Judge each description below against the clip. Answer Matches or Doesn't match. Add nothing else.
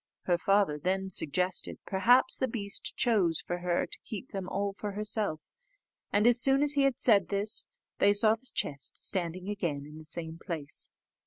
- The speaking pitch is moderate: Doesn't match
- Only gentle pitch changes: Doesn't match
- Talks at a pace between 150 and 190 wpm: Matches